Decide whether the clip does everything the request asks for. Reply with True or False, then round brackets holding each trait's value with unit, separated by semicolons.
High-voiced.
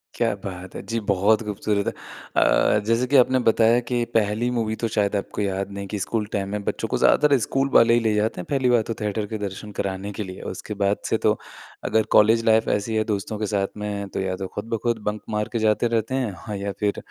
False (105 Hz)